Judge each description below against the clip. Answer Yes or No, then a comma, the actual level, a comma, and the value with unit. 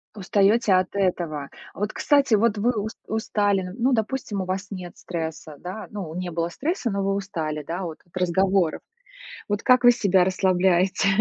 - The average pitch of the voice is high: Yes, high, 195 Hz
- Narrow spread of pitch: No, average, 3.2 semitones